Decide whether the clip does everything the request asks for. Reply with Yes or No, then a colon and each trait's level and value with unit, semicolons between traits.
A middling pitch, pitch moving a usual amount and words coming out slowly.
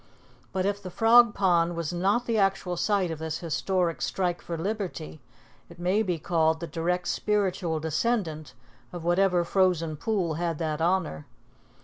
No: medium, 175 Hz; average, 3.0 semitones; average, 155 wpm